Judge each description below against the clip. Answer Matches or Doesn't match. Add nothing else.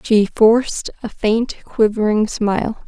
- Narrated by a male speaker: Doesn't match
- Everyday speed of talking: Doesn't match